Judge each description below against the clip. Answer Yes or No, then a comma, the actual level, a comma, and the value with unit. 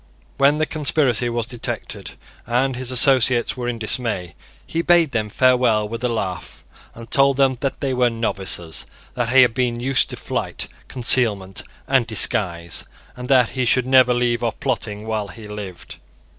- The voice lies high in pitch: No, low, 120 Hz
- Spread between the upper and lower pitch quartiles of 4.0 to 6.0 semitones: No, average, 2.9 semitones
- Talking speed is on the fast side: No, average, 170 wpm